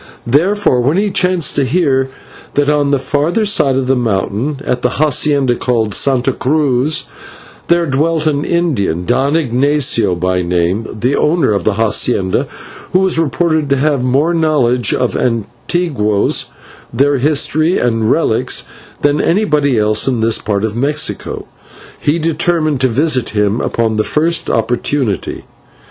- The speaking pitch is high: No, low, 135 Hz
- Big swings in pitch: No, average, 5.0 semitones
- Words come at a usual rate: Yes, average, 150 wpm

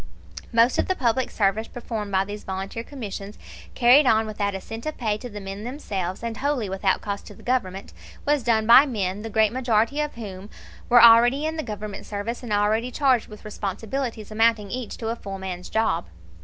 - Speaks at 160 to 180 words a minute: No, average, 200 wpm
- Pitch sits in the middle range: No, high, 220 Hz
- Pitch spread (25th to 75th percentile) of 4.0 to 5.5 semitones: No, average, 3.2 semitones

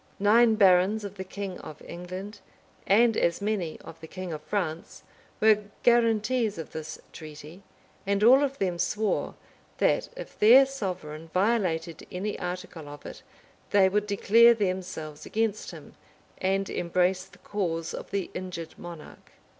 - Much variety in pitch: No, average, 3.8 semitones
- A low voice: No, high, 190 Hz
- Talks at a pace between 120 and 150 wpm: Yes, average, 145 wpm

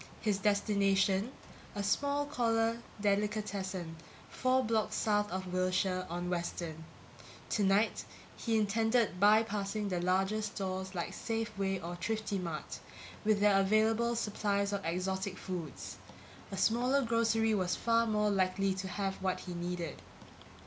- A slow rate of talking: Yes, slow, 125 wpm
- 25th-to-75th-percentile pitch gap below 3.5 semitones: Yes, average, 2.8 semitones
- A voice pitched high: Yes, high, 200 Hz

